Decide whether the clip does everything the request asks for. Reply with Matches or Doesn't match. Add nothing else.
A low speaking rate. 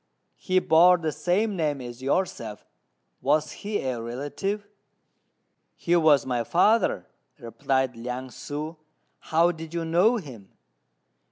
Matches